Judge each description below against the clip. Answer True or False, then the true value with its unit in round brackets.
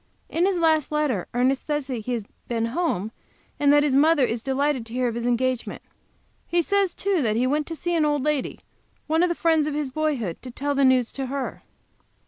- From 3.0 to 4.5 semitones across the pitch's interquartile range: True (3.8 semitones)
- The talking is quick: True (220 wpm)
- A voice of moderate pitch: False (280 Hz)